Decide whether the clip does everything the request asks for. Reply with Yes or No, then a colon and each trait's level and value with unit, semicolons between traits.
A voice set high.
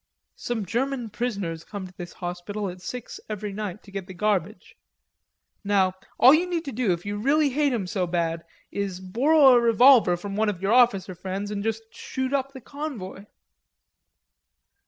Yes: high, 210 Hz